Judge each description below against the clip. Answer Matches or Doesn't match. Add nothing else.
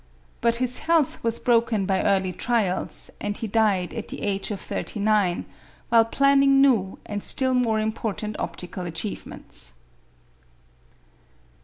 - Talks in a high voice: Matches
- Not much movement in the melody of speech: Doesn't match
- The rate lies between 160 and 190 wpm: Doesn't match